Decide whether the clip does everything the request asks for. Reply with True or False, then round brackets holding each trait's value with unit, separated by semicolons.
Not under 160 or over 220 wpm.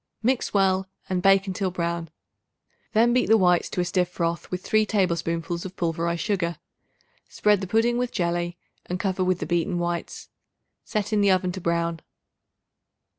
True (170 wpm)